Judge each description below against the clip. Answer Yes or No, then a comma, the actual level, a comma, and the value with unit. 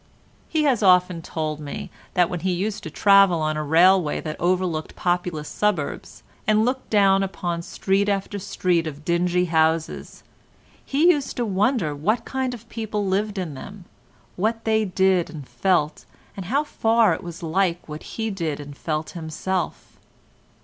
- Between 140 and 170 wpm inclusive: Yes, average, 165 wpm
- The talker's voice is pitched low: No, medium, 185 Hz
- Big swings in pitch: No, average, 4.3 semitones